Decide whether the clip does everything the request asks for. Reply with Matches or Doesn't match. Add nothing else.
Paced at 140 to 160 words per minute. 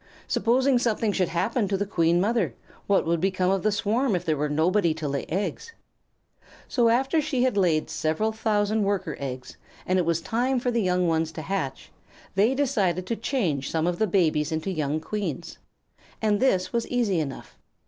Doesn't match